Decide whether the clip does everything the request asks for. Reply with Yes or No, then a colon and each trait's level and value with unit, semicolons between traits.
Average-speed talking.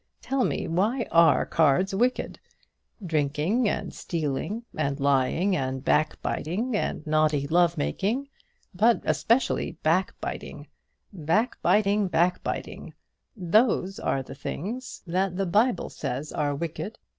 No: slow, 110 wpm